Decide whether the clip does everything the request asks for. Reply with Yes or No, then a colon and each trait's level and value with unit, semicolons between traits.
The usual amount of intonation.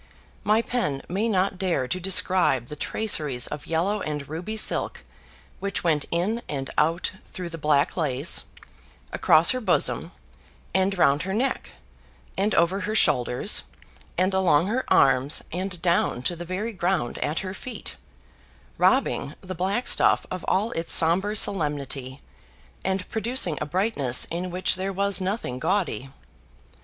Yes: average, 4.9 semitones